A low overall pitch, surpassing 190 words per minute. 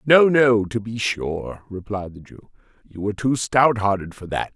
Yes: low, 110 Hz; average, 200 wpm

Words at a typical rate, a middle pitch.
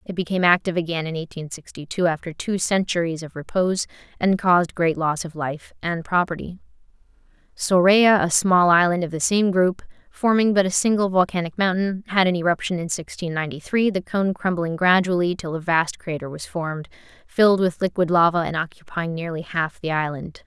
Yes: average, 180 wpm; medium, 175 Hz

